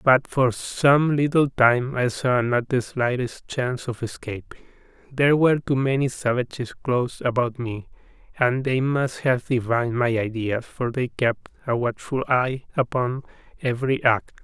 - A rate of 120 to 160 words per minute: Yes, average, 155 wpm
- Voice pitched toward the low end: Yes, low, 125 Hz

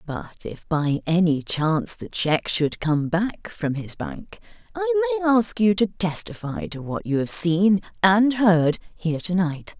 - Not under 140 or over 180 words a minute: Yes, average, 170 wpm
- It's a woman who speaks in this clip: Yes, female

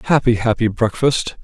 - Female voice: No, male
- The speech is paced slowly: Yes, slow, 125 wpm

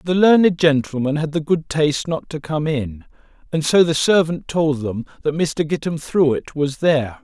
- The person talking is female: No, male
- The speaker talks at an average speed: Yes, average, 185 wpm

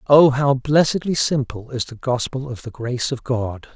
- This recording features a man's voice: Yes, male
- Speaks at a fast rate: No, average, 190 wpm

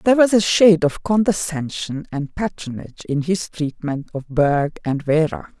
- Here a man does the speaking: No, female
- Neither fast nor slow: Yes, average, 160 wpm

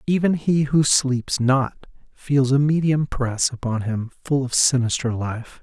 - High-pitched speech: No, low, 135 Hz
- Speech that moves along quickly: No, average, 160 wpm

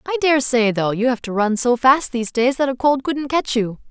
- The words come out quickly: Yes, fast, 275 wpm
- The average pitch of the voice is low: No, very high, 255 Hz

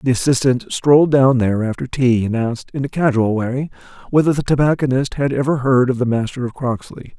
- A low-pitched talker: Yes, low, 130 Hz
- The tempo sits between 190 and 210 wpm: Yes, average, 200 wpm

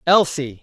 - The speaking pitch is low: No, medium, 150 Hz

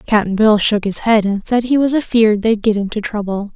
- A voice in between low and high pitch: No, high, 215 Hz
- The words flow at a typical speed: No, fast, 235 wpm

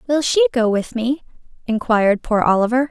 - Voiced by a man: No, female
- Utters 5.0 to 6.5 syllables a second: Yes, 5.5 syllables/s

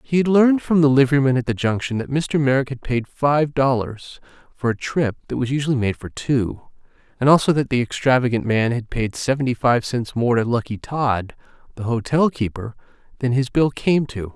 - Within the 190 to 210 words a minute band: Yes, average, 200 wpm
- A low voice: Yes, low, 130 Hz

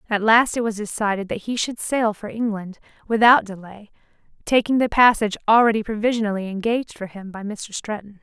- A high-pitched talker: Yes, high, 215 Hz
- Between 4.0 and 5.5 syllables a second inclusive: No, 5.8 syllables/s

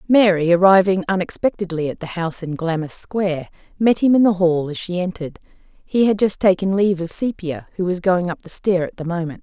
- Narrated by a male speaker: No, female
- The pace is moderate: No, fast, 210 wpm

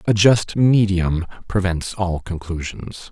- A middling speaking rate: No, slow, 115 wpm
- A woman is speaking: No, male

